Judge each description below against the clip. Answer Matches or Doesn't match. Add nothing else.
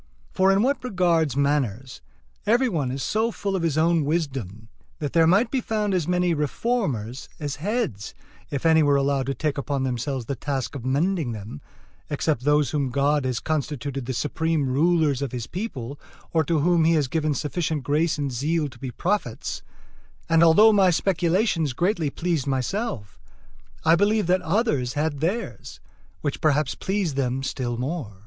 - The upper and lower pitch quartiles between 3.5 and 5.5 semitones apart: Matches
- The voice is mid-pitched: Matches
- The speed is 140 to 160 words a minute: Doesn't match